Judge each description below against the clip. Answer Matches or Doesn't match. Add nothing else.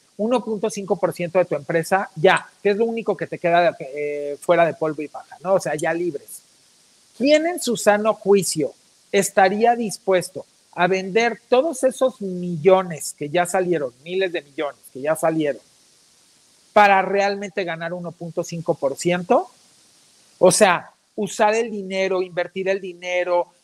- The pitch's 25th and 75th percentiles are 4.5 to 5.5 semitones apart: Doesn't match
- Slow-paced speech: Doesn't match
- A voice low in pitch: Doesn't match